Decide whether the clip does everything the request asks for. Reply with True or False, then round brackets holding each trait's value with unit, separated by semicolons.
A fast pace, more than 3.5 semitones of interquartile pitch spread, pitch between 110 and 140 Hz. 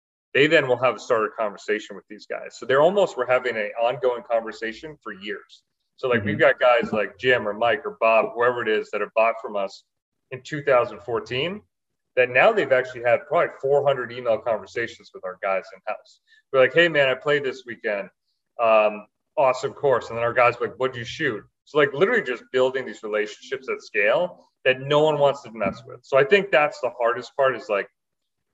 True (210 wpm; 3.9 semitones; 125 Hz)